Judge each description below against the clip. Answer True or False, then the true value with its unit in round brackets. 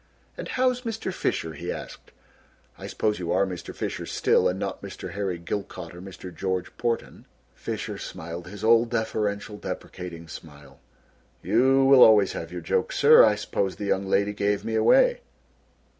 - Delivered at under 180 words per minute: True (165 wpm)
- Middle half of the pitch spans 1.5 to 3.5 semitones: False (4.2 semitones)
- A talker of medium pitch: False (100 Hz)